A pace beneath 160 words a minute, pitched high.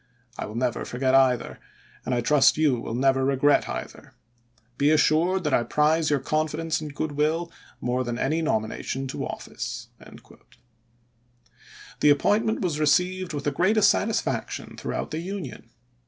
No: average, 145 wpm; medium, 150 Hz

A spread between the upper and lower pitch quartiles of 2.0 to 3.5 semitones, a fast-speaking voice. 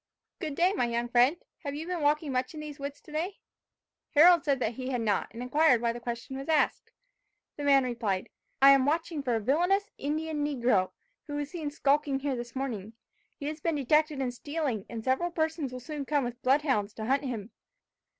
No: average, 3.9 semitones; fast, 210 wpm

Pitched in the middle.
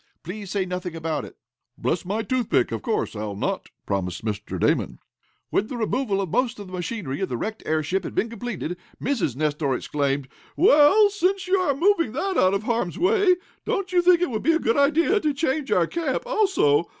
No: high, 225 Hz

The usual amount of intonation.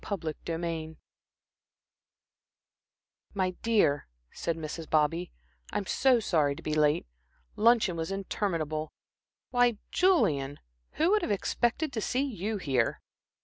No: wide, 6.6 semitones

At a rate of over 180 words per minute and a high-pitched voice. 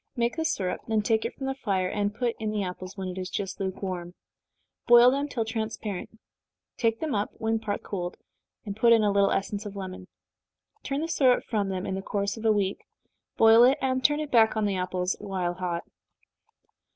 Yes: fast, 205 wpm; high, 210 Hz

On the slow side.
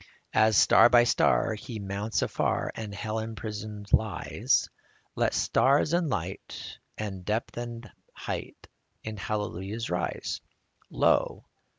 Yes: slow, 115 wpm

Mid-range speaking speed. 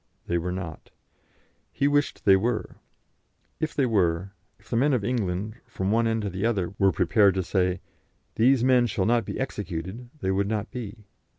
Yes: average, 185 wpm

